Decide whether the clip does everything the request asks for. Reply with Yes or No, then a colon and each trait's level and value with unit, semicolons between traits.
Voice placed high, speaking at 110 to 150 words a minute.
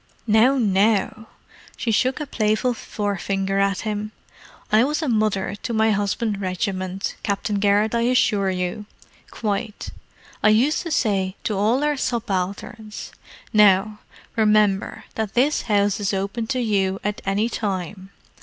Yes: high, 210 Hz; average, 140 wpm